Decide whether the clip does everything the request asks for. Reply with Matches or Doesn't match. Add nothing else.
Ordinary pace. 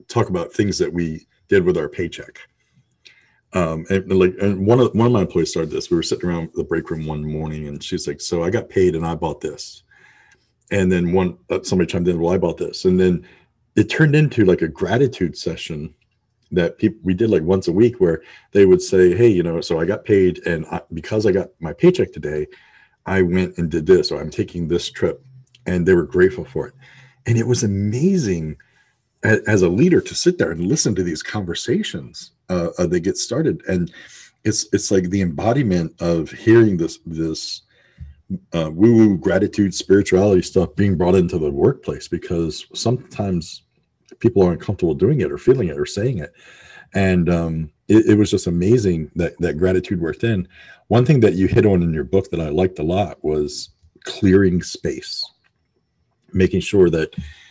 Matches